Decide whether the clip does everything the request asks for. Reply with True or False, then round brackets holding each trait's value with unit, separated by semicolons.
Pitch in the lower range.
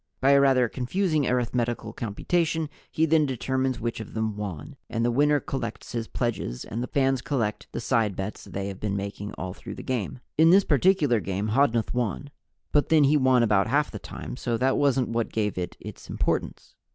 True (125 Hz)